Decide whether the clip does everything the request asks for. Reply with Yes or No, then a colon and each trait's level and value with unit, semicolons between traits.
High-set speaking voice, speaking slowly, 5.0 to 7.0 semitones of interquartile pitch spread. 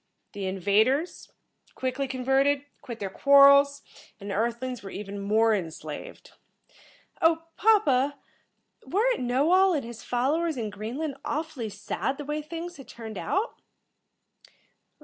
Yes: very high, 265 Hz; slow, 130 wpm; wide, 5.6 semitones